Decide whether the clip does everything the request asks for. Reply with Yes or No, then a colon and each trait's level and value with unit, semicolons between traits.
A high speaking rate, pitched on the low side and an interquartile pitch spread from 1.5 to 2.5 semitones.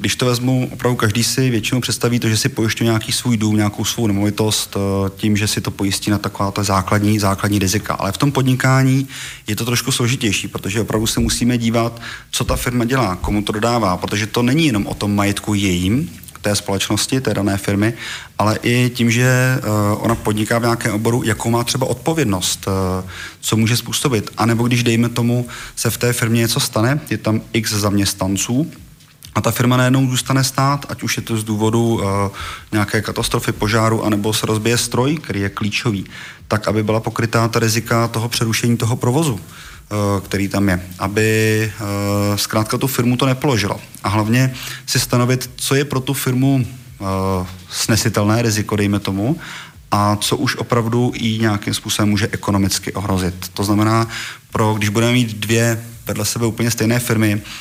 No: fast, 180 wpm; low, 115 Hz; average, 2.9 semitones